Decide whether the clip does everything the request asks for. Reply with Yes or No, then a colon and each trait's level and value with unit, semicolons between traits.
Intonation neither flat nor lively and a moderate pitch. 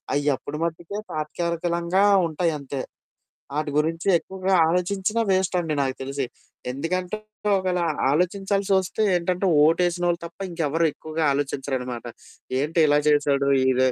Yes: average, 3.8 semitones; medium, 165 Hz